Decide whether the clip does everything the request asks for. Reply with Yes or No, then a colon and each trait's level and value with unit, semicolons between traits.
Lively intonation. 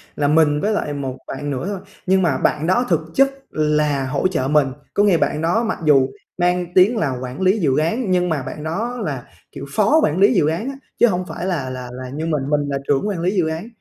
No: average, 4.9 semitones